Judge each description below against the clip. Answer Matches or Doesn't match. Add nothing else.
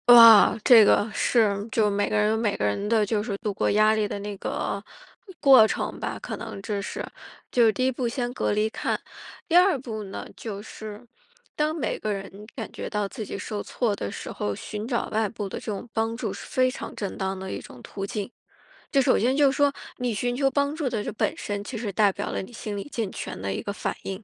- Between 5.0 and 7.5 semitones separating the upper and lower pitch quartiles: Doesn't match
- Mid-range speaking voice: Doesn't match